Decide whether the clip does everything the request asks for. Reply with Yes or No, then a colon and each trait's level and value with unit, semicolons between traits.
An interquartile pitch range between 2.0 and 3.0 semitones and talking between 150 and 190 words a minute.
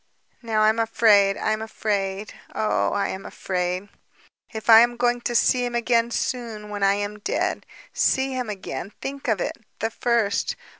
Yes: average, 2.7 semitones; average, 170 wpm